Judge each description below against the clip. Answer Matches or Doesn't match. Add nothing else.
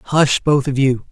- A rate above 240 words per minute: Doesn't match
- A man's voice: Matches